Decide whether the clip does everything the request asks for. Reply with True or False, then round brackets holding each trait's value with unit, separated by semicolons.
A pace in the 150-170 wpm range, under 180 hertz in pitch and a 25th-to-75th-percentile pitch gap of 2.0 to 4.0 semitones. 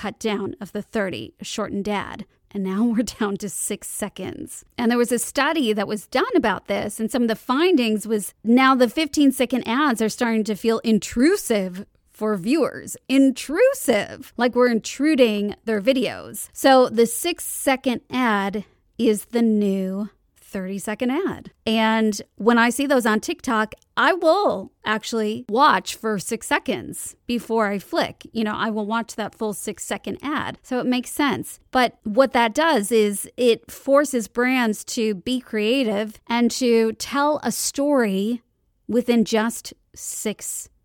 False (160 wpm; 230 Hz; 3.1 semitones)